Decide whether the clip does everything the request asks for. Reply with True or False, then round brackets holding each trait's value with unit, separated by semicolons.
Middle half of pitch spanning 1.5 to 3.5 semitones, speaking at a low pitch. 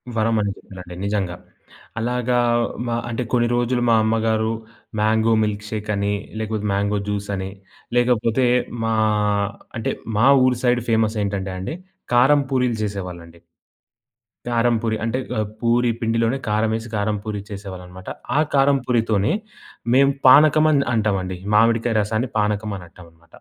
True (2.8 semitones; 110 Hz)